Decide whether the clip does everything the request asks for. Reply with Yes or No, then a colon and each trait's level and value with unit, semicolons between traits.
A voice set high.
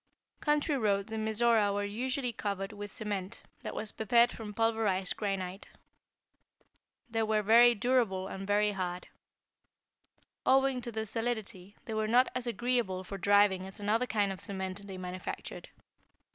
Yes: high, 210 Hz